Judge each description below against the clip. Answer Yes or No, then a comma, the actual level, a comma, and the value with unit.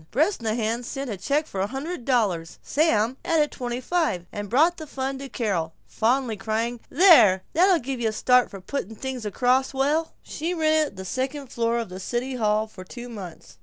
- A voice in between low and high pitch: No, high, 245 Hz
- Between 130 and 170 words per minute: No, average, 195 wpm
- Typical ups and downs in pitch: Yes, average, 4.6 semitones